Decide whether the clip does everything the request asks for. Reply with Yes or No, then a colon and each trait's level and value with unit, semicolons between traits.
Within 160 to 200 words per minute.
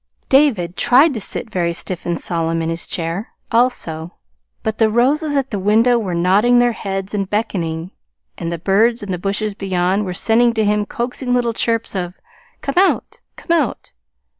Yes: average, 180 wpm